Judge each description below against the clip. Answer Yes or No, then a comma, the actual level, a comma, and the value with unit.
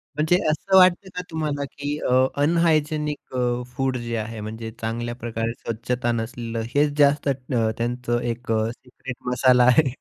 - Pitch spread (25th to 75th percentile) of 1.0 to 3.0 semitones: No, average, 4.1 semitones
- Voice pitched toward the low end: Yes, low, 125 Hz